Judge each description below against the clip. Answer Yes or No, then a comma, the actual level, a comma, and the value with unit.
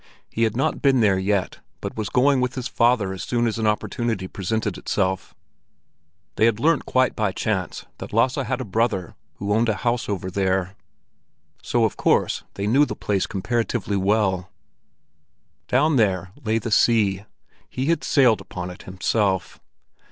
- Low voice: Yes, low, 110 Hz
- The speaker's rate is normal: Yes, average, 165 wpm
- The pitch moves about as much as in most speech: Yes, average, 4.1 semitones